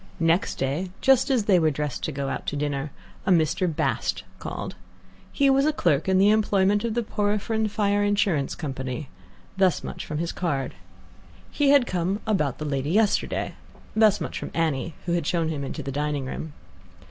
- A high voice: No, medium, 175 Hz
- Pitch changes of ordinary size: No, wide, 5.9 semitones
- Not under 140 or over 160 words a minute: No, average, 185 wpm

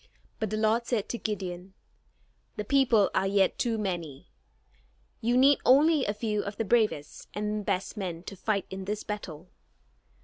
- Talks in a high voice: Yes, high, 210 Hz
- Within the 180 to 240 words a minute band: No, average, 165 wpm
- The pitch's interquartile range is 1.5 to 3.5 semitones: Yes, average, 3.0 semitones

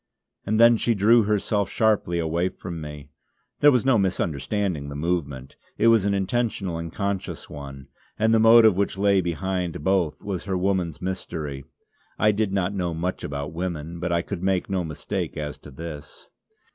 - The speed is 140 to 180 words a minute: Yes, average, 175 wpm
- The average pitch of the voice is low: Yes, very low, 90 Hz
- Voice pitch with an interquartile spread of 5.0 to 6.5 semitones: No, average, 3.9 semitones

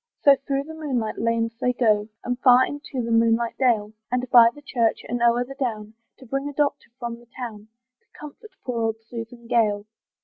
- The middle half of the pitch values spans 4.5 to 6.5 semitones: No, narrow, 2.6 semitones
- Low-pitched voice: No, high, 240 Hz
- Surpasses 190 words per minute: Yes, average, 200 wpm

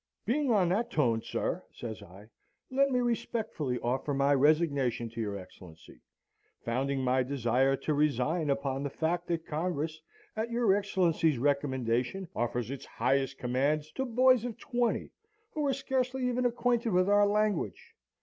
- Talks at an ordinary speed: Yes, average, 150 wpm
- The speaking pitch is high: No, medium, 155 Hz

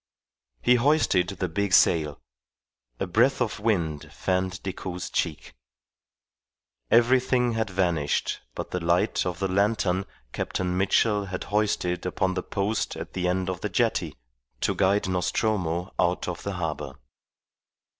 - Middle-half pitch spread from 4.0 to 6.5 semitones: No, average, 2.8 semitones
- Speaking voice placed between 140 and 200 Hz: No, very low, 95 Hz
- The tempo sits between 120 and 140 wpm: Yes, slow, 135 wpm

